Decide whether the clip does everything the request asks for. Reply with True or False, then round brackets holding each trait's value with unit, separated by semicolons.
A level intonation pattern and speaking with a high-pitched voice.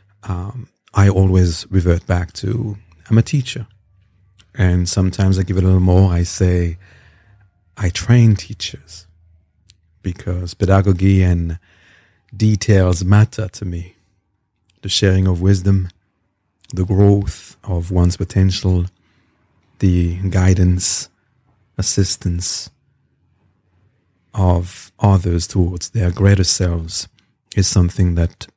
False (2.0 semitones; 95 Hz)